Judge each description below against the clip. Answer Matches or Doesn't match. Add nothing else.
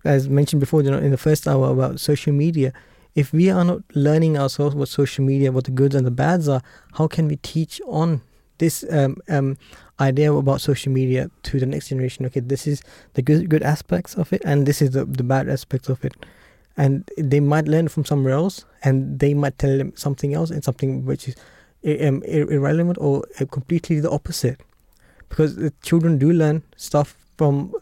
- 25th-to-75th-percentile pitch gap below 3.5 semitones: Matches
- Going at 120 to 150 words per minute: Doesn't match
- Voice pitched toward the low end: Doesn't match